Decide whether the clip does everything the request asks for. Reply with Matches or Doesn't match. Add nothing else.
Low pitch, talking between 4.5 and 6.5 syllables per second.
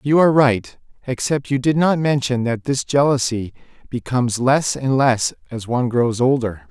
Matches